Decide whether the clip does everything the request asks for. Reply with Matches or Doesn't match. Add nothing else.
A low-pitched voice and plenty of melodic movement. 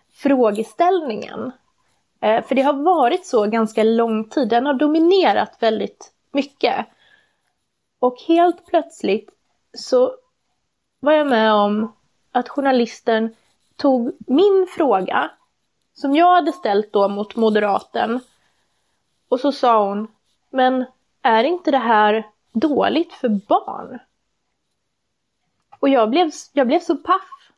Doesn't match